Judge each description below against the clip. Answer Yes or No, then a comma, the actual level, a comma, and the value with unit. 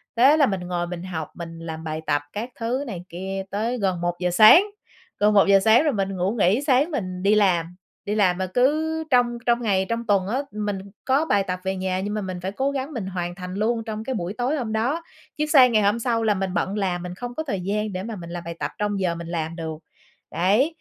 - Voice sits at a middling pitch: No, high, 200 Hz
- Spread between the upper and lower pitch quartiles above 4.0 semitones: Yes, average, 4.8 semitones